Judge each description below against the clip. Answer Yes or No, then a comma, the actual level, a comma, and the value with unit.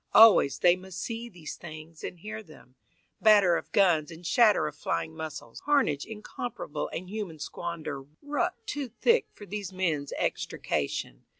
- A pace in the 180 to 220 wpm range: No, average, 155 wpm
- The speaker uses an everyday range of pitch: No, wide, 5.7 semitones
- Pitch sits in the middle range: Yes, medium, 180 Hz